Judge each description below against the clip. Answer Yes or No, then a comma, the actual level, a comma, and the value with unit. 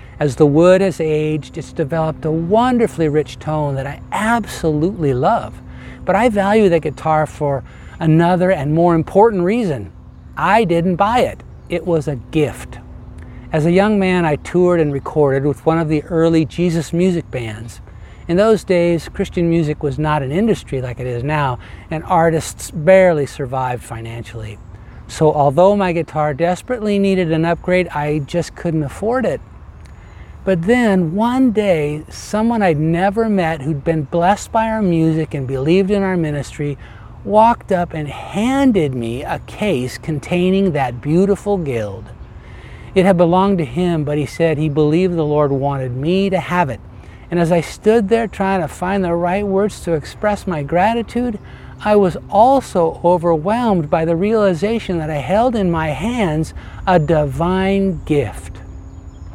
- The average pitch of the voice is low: No, medium, 165 Hz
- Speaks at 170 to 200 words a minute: No, average, 160 wpm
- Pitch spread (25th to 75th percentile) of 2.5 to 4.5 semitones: No, average, 5.1 semitones